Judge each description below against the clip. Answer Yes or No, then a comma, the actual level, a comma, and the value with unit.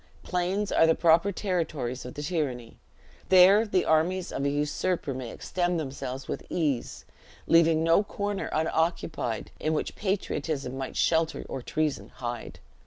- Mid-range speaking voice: Yes, medium, 160 Hz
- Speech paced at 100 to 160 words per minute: Yes, average, 140 wpm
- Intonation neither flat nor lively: Yes, average, 4.7 semitones